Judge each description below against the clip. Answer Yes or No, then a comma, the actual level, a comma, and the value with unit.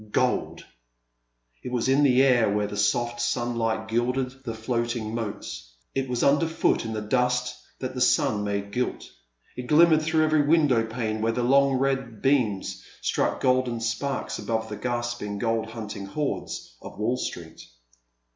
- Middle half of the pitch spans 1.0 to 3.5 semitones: Yes, average, 3.1 semitones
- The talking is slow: No, average, 165 wpm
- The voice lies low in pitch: Yes, low, 120 Hz